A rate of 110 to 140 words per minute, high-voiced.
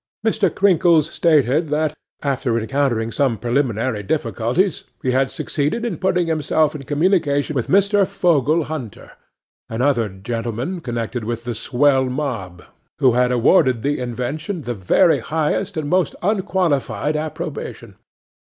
No: slow, 135 wpm; medium, 140 Hz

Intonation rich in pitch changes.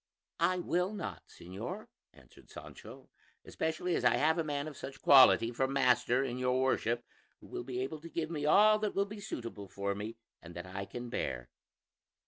Yes: wide, 6.2 semitones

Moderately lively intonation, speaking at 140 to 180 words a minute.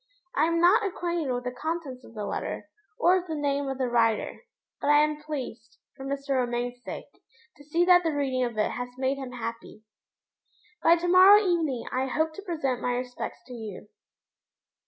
No: average, 5.0 semitones; average, 195 wpm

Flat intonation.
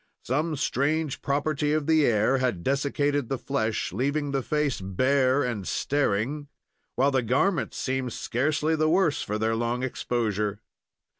No: average, 3.7 semitones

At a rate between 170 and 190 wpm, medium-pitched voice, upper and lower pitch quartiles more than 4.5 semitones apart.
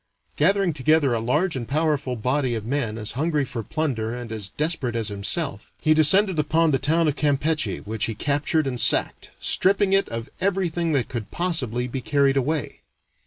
Yes: average, 180 wpm; medium, 145 Hz; average, 5.1 semitones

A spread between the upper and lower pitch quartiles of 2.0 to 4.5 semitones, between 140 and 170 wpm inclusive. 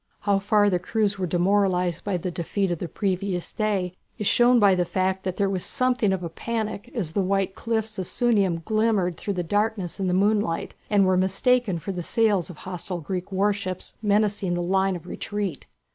No: narrow, 2.5 semitones; average, 200 wpm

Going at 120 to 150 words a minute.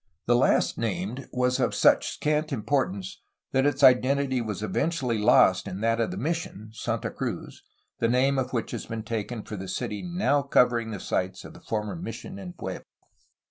No: average, 180 wpm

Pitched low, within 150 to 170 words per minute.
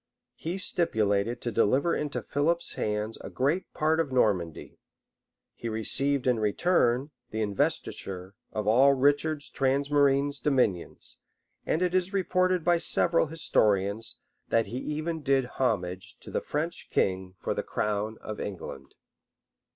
No: low, 130 Hz; slow, 135 wpm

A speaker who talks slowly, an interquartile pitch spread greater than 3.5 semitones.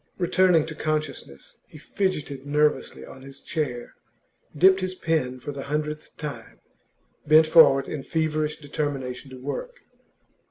No: slow, 130 wpm; average, 2.8 semitones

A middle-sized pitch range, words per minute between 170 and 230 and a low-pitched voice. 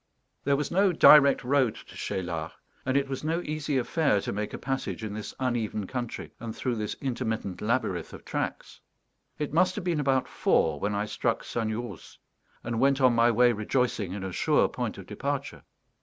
Yes: average, 4.6 semitones; average, 185 wpm; low, 120 Hz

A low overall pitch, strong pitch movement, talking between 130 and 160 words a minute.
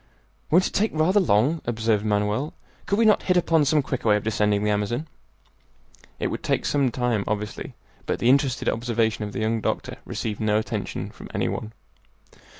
No: low, 115 Hz; wide, 5.8 semitones; average, 185 wpm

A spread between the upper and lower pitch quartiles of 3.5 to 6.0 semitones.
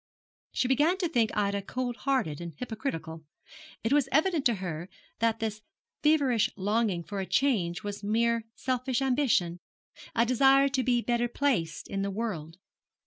Yes: average, 5.1 semitones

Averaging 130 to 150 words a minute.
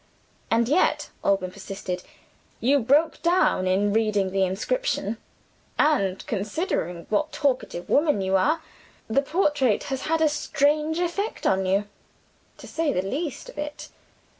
Yes: average, 140 wpm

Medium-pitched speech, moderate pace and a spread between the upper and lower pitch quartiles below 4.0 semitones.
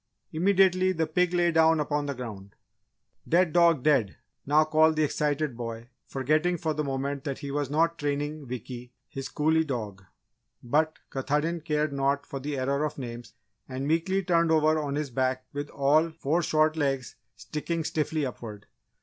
Yes: medium, 150 Hz; average, 165 wpm; average, 2.9 semitones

